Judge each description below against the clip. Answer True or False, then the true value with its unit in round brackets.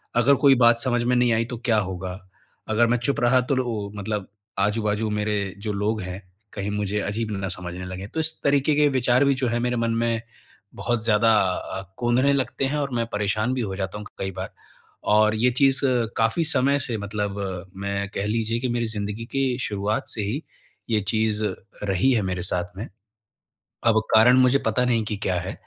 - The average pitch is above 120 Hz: False (110 Hz)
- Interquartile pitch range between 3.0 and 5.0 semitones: True (3.3 semitones)